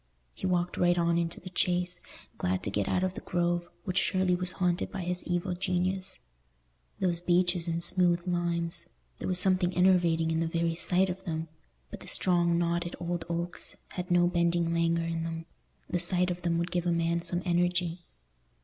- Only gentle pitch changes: Yes, narrow, 1.1 semitones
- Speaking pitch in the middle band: Yes, medium, 175 Hz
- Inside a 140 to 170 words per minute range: No, average, 185 wpm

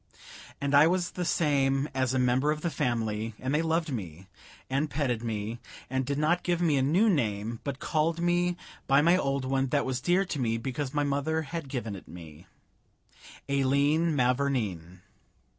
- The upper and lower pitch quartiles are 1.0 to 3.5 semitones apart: No, average, 4.3 semitones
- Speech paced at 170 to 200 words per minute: Yes, average, 180 wpm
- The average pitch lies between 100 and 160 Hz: Yes, medium, 140 Hz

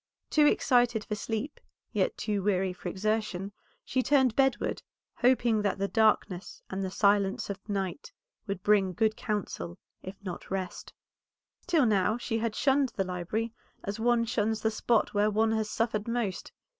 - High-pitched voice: Yes, high, 215 Hz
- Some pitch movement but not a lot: Yes, average, 3.0 semitones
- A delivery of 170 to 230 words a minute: No, average, 160 wpm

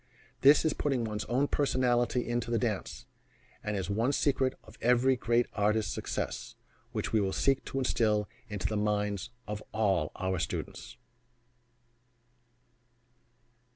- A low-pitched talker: Yes, low, 115 Hz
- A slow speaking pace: Yes, slow, 130 wpm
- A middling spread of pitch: Yes, average, 3.4 semitones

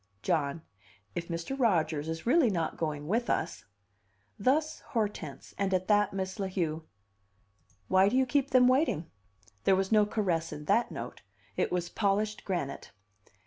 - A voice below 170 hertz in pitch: No, high, 190 Hz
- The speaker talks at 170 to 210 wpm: No, average, 160 wpm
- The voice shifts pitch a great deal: Yes, wide, 5.7 semitones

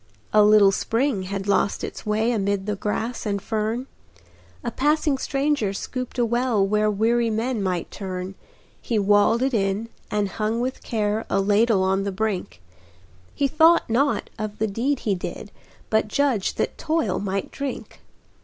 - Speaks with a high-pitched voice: Yes, high, 215 Hz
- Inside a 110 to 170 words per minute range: Yes, average, 165 wpm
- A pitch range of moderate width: Yes, average, 3.4 semitones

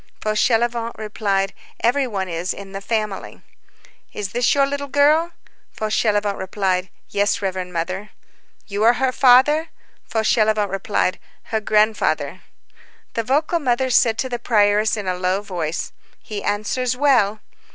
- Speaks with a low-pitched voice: No, high, 215 Hz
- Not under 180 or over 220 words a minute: No, slow, 135 wpm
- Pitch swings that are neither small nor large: Yes, average, 3.8 semitones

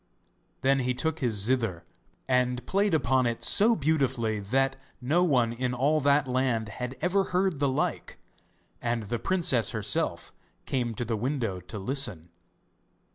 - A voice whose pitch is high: No, low, 125 Hz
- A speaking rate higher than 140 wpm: Yes, average, 150 wpm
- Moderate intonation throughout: Yes, average, 3.6 semitones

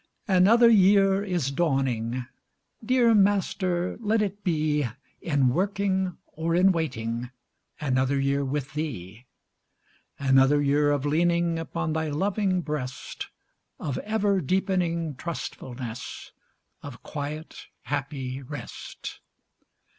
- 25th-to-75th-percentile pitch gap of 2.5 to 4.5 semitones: No, wide, 5.6 semitones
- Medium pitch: Yes, medium, 155 Hz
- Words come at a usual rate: No, slow, 100 wpm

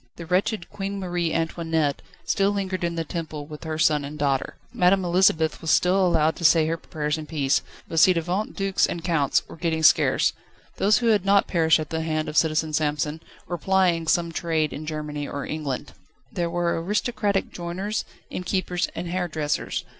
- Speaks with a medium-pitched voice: Yes, medium, 165 Hz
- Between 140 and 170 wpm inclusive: No, average, 185 wpm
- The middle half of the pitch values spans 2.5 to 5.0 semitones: Yes, average, 2.9 semitones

